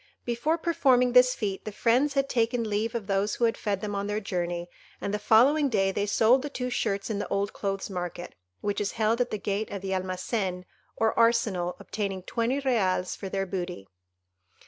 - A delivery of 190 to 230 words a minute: Yes, average, 200 wpm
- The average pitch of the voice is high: Yes, high, 210 Hz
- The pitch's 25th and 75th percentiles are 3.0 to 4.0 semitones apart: Yes, average, 3.5 semitones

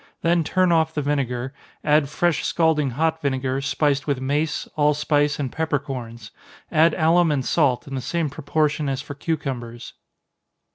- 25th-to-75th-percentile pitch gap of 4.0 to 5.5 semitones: No, average, 3.0 semitones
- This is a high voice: No, medium, 145 Hz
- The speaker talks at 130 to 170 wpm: Yes, average, 150 wpm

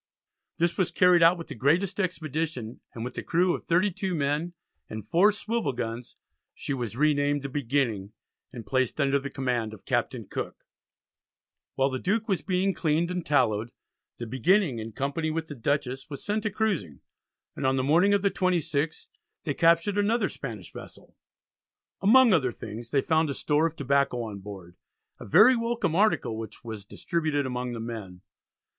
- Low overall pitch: No, medium, 145 Hz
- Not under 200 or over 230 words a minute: No, average, 175 wpm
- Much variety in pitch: Yes, wide, 6.5 semitones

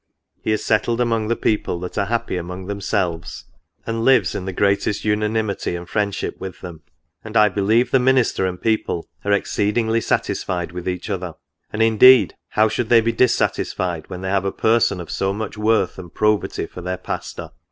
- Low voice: Yes, low, 100 Hz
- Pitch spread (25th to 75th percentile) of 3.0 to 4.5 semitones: Yes, average, 3.4 semitones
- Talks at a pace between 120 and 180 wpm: No, average, 195 wpm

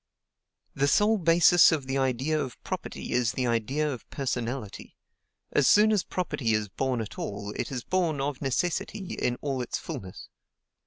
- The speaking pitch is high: No, low, 135 Hz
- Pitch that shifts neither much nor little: Yes, average, 4.7 semitones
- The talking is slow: No, average, 165 wpm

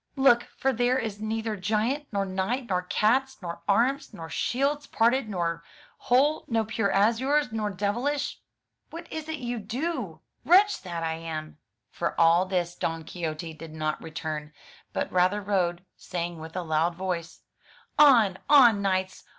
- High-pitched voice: Yes, high, 200 Hz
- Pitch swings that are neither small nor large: No, wide, 6.3 semitones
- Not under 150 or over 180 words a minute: Yes, average, 155 wpm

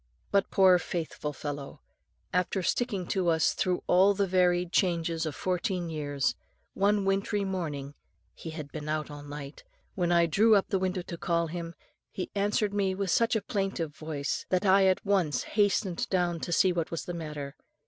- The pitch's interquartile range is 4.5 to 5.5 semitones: No, average, 3.3 semitones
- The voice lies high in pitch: No, medium, 180 Hz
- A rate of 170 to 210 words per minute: Yes, average, 180 wpm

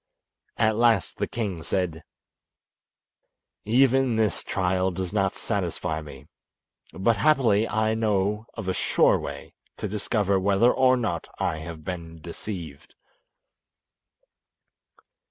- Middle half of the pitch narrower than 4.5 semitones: Yes, average, 3.9 semitones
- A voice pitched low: Yes, low, 100 Hz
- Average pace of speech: No, slow, 115 wpm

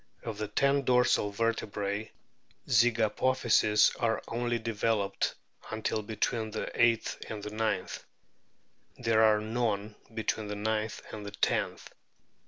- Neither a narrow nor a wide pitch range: No, narrow, 1.6 semitones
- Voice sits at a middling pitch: No, low, 110 Hz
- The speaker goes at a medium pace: No, slow, 110 wpm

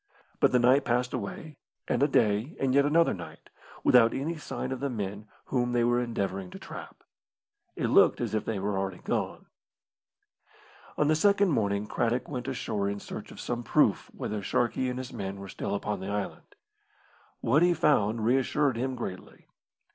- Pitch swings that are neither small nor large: Yes, average, 4.6 semitones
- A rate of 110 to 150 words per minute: No, average, 180 wpm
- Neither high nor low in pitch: No, low, 120 Hz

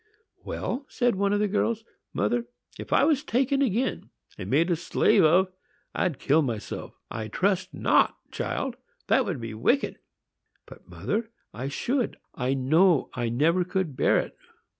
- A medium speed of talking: Yes, average, 155 wpm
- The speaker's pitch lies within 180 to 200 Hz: Yes, medium, 185 Hz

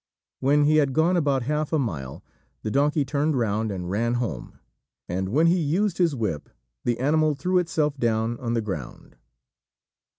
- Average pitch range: No, wide, 5.7 semitones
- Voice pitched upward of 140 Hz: No, low, 135 Hz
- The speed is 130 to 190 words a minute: Yes, average, 170 wpm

